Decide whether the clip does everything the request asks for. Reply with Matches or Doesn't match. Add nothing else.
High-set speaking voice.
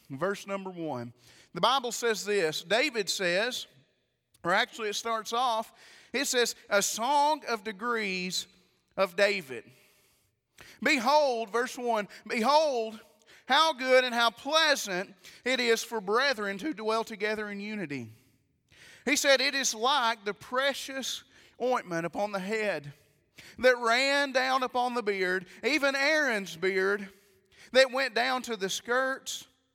Matches